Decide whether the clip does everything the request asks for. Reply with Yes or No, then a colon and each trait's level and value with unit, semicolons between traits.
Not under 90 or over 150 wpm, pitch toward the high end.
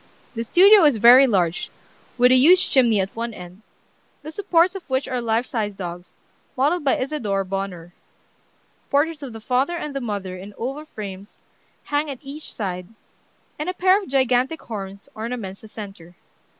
No: average, 165 wpm; high, 240 Hz